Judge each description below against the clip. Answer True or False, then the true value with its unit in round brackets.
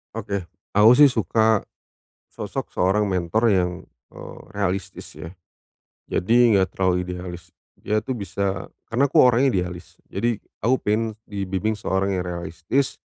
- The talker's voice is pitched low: True (100 Hz)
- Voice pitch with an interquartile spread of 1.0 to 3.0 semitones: False (3.6 semitones)